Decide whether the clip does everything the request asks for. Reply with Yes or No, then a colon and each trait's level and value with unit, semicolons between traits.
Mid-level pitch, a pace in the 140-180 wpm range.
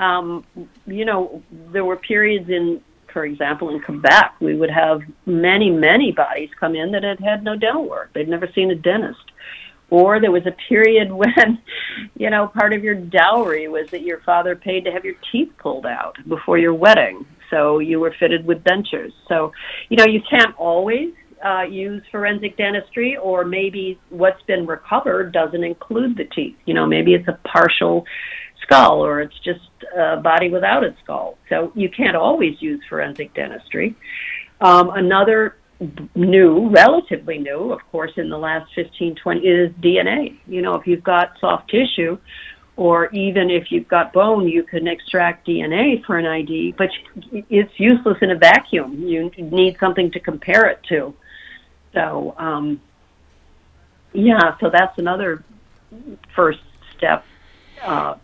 Yes: medium, 180 Hz; average, 165 wpm